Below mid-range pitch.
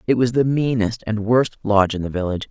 Yes: low, 110 Hz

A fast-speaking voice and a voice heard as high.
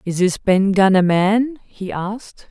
No: average, 190 wpm; high, 200 Hz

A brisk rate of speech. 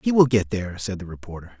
Yes: fast, 265 wpm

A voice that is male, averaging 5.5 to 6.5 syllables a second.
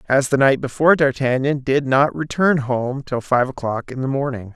No: male; 5.0 syllables/s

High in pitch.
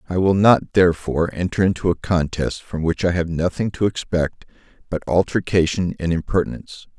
No: very low, 90 Hz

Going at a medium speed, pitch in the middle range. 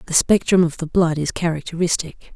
Yes: average, 180 wpm; medium, 170 Hz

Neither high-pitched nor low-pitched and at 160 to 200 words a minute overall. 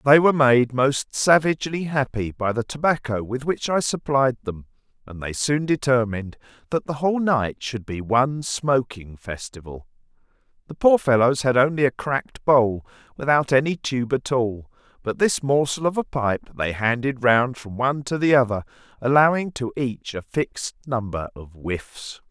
No: low, 130 Hz; average, 165 wpm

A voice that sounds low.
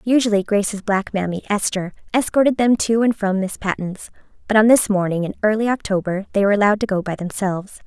No: high, 205 Hz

